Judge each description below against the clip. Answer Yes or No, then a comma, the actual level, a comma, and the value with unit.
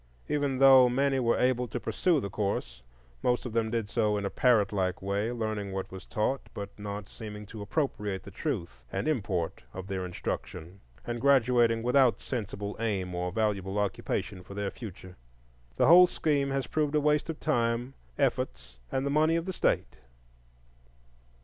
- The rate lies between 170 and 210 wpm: Yes, average, 175 wpm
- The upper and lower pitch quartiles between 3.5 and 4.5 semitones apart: No, average, 5.2 semitones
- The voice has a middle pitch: No, low, 110 Hz